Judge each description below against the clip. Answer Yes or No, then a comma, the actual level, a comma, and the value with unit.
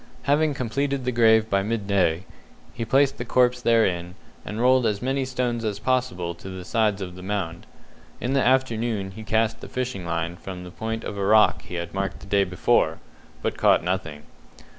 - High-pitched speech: No, low, 110 Hz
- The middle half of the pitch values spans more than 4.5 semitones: Yes, average, 4.9 semitones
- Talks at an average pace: Yes, average, 190 wpm